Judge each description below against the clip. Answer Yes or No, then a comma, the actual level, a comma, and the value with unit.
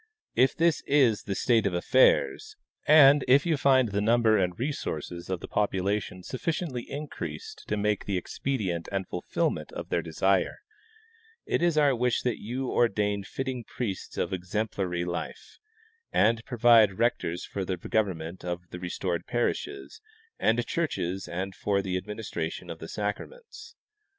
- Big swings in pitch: Yes, wide, 5.8 semitones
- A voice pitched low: Yes, low, 105 Hz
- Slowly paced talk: No, average, 145 wpm